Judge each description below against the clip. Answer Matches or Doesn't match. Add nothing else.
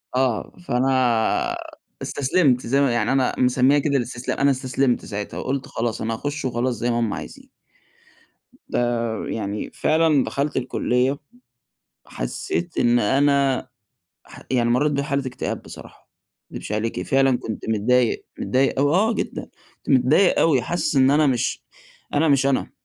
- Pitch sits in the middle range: Doesn't match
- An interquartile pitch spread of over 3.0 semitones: Doesn't match